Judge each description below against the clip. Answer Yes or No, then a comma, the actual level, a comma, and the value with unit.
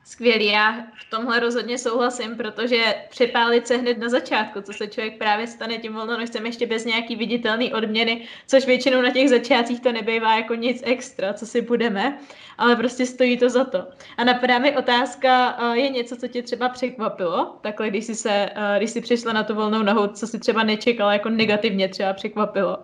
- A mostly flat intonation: Yes, narrow, 2.2 semitones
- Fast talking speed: Yes, fast, 190 wpm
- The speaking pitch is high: Yes, high, 235 Hz